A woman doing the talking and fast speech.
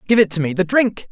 No: male; fast, 320 wpm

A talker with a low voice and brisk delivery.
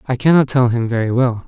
Yes: low, 125 Hz; fast, 245 wpm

